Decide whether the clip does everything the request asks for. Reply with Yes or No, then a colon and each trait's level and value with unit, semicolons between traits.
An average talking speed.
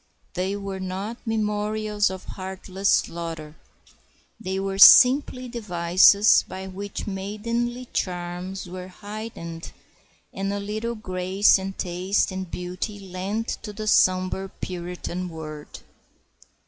No: slow, 110 wpm